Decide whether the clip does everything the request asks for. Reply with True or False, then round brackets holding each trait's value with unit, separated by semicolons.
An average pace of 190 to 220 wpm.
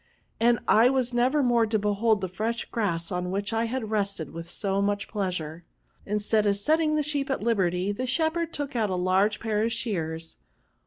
True (195 wpm)